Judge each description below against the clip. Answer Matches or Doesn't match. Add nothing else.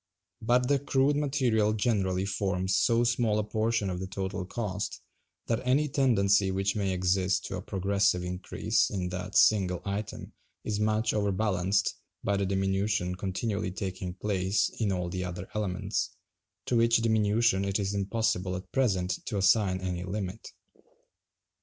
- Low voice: Matches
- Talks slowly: Doesn't match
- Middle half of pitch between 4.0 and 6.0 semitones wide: Doesn't match